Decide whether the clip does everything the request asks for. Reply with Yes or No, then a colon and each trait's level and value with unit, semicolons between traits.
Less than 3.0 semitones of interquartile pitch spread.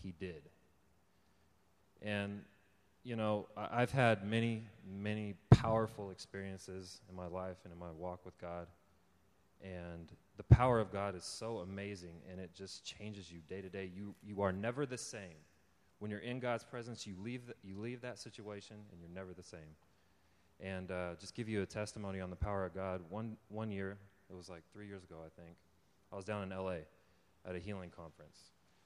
Yes: narrow, 2.6 semitones